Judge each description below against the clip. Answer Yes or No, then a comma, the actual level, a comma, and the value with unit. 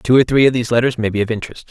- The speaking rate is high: Yes, fast, 350 wpm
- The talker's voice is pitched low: Yes, low, 120 Hz